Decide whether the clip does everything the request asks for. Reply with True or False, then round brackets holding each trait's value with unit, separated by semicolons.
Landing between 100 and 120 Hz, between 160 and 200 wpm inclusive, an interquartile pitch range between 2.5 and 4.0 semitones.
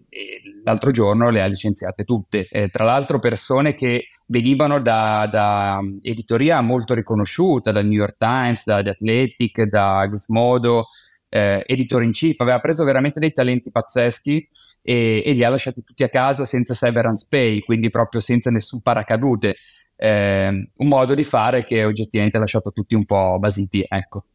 True (115 Hz; 165 wpm; 3.7 semitones)